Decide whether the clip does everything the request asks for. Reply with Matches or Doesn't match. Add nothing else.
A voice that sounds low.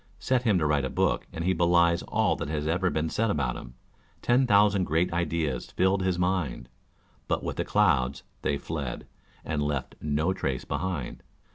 Matches